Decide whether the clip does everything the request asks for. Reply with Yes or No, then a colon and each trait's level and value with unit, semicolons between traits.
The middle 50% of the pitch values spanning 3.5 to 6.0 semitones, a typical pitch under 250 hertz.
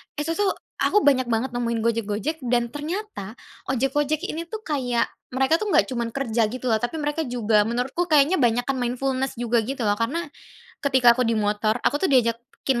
No: average, 4.1 semitones; very high, 255 Hz